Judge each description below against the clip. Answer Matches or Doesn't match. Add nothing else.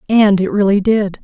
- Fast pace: Doesn't match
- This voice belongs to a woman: Matches